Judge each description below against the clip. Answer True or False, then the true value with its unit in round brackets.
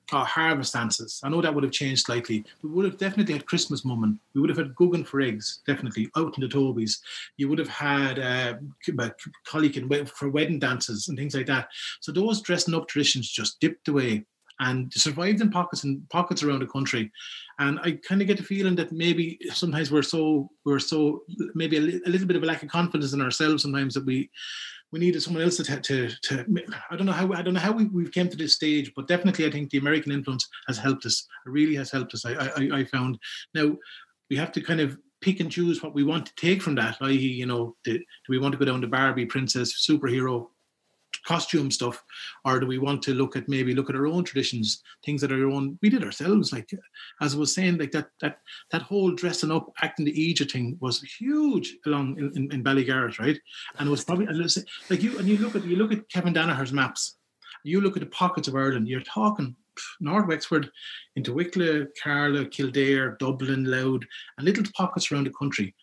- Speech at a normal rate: False (225 wpm)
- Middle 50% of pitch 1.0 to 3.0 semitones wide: False (4.2 semitones)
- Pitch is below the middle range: False (145 Hz)